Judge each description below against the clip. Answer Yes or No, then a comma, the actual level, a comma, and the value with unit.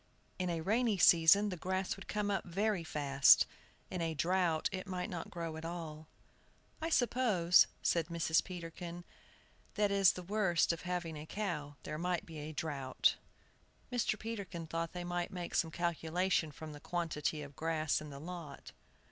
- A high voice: No, medium, 170 Hz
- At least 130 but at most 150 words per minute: No, average, 170 wpm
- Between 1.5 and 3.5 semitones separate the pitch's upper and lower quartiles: Yes, average, 2.9 semitones